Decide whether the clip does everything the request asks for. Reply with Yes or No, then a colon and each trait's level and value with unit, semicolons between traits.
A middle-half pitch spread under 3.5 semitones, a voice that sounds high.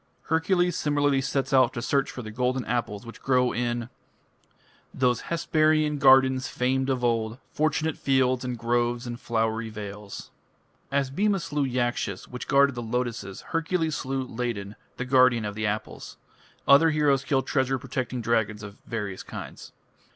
No: average, 3.1 semitones; low, 125 Hz